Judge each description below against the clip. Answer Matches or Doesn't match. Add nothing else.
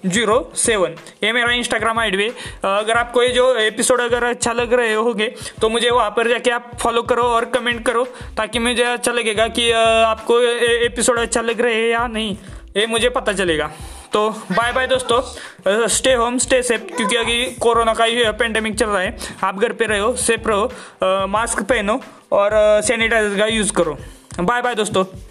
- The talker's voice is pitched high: Matches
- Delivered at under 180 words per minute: Doesn't match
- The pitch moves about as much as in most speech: Doesn't match